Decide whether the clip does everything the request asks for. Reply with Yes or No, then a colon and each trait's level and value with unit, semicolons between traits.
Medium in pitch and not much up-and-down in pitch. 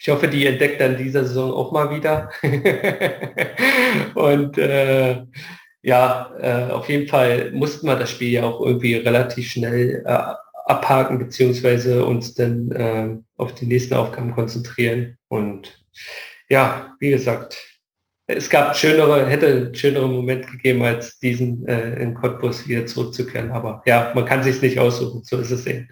No: low, 125 Hz; narrow, 1.8 semitones